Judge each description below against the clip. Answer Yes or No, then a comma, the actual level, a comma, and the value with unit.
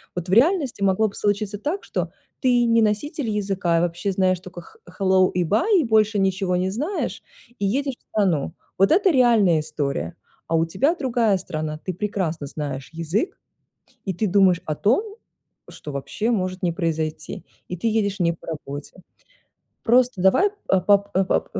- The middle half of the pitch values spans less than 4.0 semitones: No, average, 4.6 semitones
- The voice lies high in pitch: Yes, high, 195 Hz